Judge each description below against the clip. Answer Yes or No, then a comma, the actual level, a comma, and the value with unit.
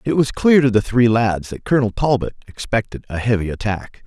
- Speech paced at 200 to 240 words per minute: Yes, fast, 205 wpm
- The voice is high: No, low, 115 Hz